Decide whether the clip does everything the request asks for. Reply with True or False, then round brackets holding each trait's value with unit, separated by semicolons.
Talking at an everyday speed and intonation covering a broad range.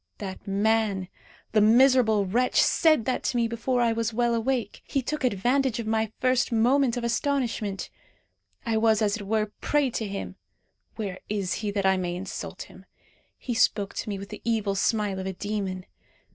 False (185 wpm; 3.2 semitones)